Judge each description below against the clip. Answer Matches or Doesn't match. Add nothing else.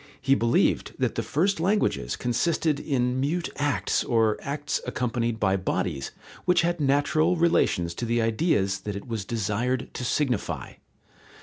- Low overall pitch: Matches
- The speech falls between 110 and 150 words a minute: Matches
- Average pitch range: Doesn't match